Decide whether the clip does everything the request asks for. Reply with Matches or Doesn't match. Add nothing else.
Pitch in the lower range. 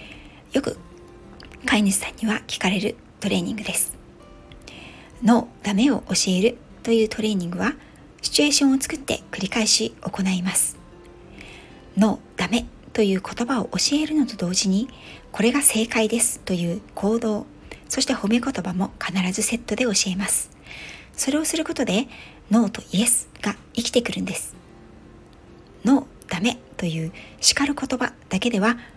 Doesn't match